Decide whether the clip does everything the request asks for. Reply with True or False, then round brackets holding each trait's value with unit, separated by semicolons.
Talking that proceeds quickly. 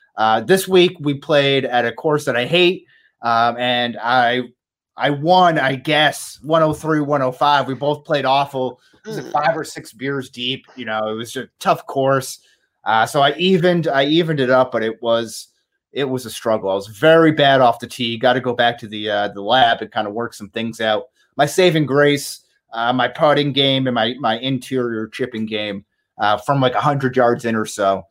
True (220 wpm)